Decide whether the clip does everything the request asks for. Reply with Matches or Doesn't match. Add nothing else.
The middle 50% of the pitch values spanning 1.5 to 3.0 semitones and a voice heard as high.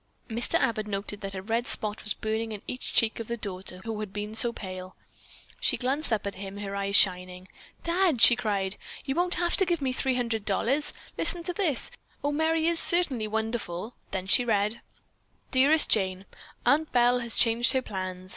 Doesn't match